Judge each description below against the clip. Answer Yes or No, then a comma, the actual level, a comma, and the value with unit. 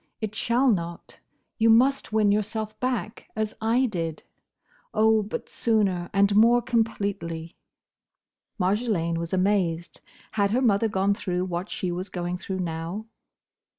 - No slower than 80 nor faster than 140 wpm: Yes, slow, 135 wpm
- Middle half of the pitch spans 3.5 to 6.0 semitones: Yes, average, 3.8 semitones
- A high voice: Yes, high, 205 Hz